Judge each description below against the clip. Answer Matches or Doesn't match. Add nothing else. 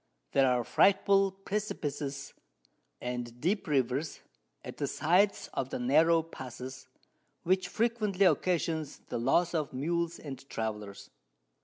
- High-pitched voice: Doesn't match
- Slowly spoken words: Matches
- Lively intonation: Matches